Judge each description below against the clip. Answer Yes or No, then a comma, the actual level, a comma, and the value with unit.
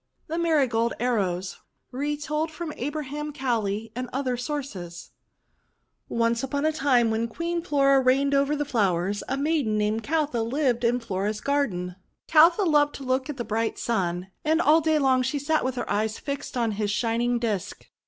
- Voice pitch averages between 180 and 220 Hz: No, very high, 255 Hz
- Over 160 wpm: Yes, average, 170 wpm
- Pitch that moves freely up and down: No, average, 4.7 semitones